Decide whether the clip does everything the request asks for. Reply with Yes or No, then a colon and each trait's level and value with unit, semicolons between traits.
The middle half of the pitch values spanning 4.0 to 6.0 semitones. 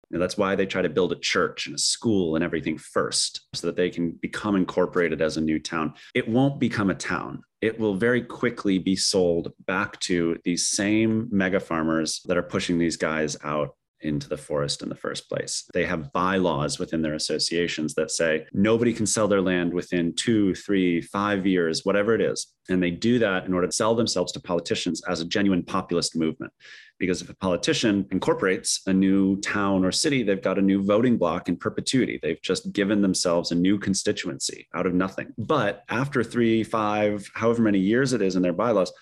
No: average, 3.2 semitones